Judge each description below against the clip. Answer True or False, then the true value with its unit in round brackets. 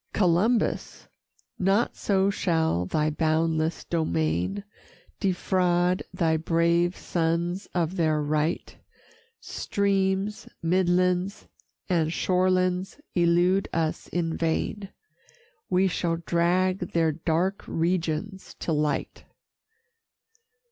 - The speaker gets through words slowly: True (85 wpm)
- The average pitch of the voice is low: False (175 Hz)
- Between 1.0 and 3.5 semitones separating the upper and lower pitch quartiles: True (2.4 semitones)